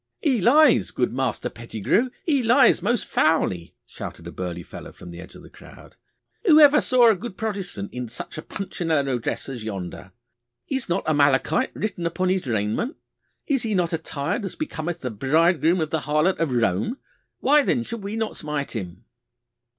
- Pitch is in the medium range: Yes, medium, 165 Hz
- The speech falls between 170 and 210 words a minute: Yes, average, 180 wpm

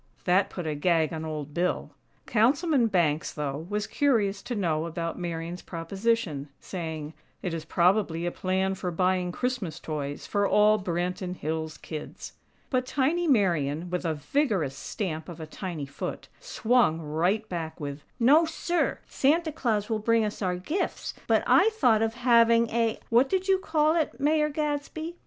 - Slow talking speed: No, average, 165 wpm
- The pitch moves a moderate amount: No, wide, 6.9 semitones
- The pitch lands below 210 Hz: Yes, high, 190 Hz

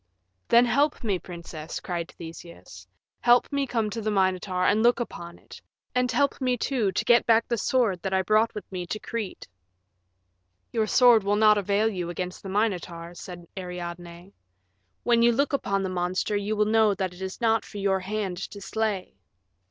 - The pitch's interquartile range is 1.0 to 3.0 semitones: No, average, 3.9 semitones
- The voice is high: Yes, high, 200 Hz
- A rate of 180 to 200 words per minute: Yes, average, 190 wpm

